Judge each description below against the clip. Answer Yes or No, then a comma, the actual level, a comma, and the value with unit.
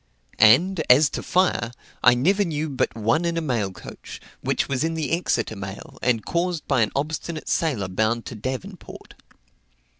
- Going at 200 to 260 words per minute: No, average, 170 wpm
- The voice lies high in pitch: No, medium, 140 Hz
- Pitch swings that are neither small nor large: No, wide, 6.3 semitones